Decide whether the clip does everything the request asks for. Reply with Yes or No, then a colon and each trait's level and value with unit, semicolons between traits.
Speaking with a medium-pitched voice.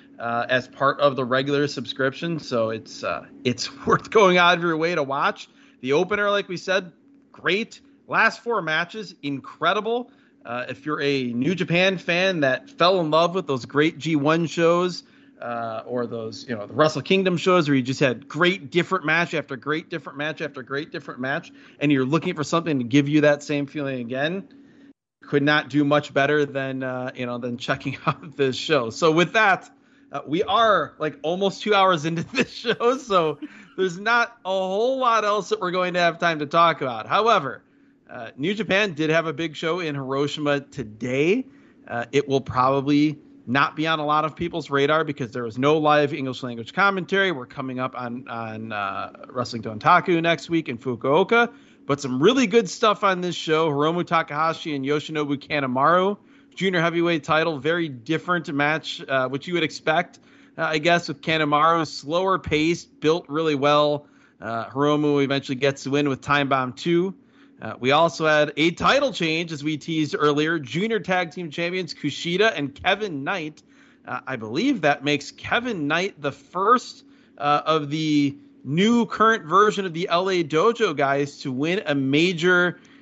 Yes: medium, 155 Hz